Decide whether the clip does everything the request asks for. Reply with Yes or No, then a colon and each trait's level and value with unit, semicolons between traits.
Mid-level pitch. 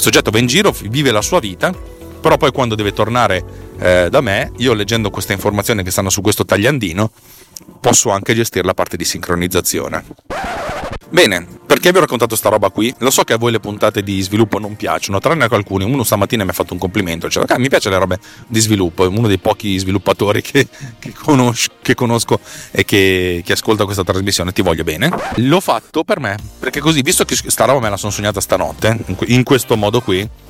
No: low, 105 Hz